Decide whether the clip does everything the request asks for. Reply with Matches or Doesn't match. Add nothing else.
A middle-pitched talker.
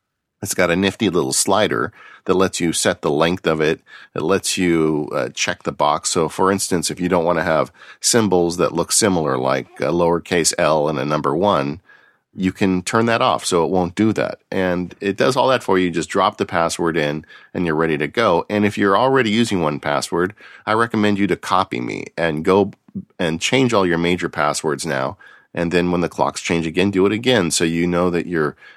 Doesn't match